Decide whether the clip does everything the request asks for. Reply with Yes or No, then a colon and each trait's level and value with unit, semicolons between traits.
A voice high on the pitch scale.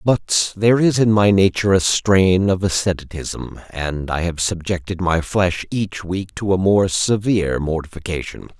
No: very low, 95 Hz